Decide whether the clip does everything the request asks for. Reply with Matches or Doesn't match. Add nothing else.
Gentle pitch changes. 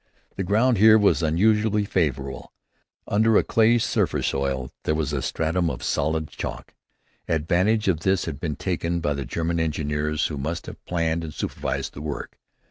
Doesn't match